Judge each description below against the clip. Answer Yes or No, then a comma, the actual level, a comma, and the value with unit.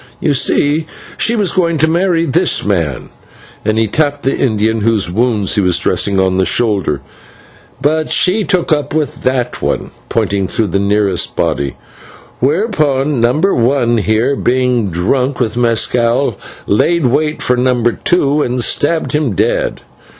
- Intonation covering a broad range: Yes, wide, 6.1 semitones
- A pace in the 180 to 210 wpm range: No, average, 150 wpm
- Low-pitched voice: Yes, low, 125 Hz